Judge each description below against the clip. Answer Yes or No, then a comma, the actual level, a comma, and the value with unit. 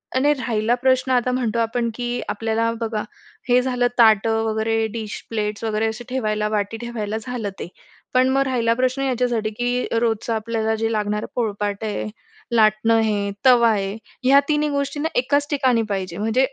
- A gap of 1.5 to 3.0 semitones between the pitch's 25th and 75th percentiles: Yes, narrow, 2.6 semitones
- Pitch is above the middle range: Yes, high, 230 Hz